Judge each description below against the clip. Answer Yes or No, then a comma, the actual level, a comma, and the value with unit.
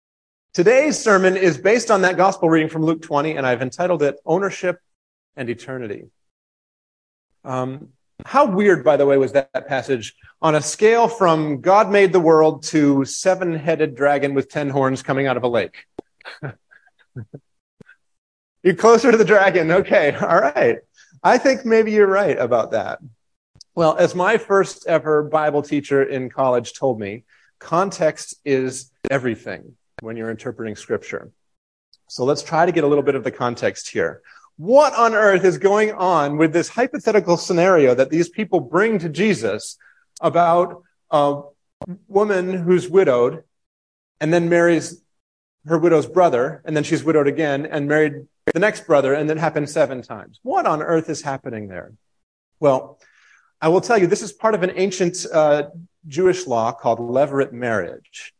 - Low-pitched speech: No, medium, 155 Hz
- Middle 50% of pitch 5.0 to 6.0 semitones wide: Yes, average, 5.3 semitones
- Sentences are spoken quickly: No, average, 160 wpm